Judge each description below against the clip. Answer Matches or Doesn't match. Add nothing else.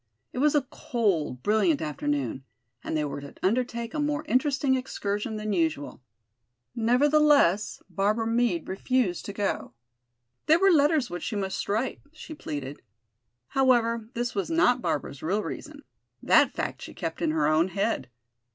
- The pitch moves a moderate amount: Doesn't match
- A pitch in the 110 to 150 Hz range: Doesn't match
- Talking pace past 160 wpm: Doesn't match